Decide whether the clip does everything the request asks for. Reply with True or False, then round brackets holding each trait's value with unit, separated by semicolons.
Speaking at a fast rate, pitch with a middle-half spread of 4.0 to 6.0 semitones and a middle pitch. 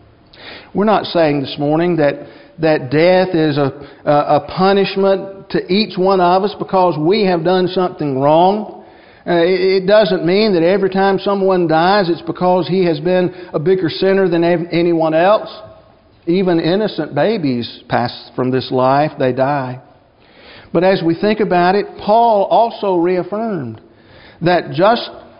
False (145 wpm; 4.4 semitones; 175 Hz)